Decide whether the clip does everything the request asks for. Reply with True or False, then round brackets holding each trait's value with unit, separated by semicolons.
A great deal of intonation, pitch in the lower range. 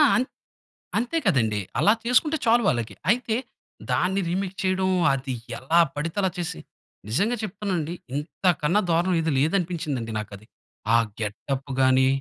False (6.9 semitones; 170 Hz)